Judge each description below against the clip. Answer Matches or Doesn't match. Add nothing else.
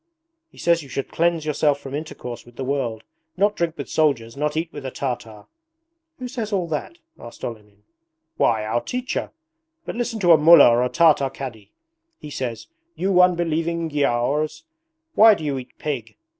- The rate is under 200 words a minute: Matches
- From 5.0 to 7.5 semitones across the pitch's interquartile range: Matches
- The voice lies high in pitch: Doesn't match